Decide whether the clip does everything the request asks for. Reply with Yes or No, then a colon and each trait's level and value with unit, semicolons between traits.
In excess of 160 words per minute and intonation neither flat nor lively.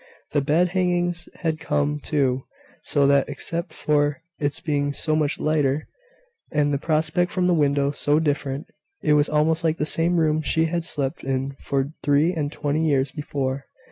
No: average, 175 wpm; narrow, 2.1 semitones